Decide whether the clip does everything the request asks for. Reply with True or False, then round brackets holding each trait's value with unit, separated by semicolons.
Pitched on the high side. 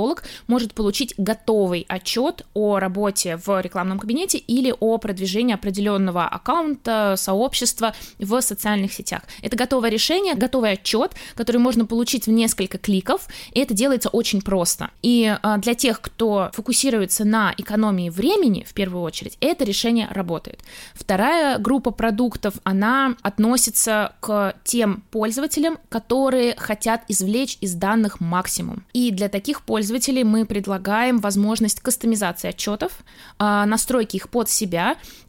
True (220 Hz)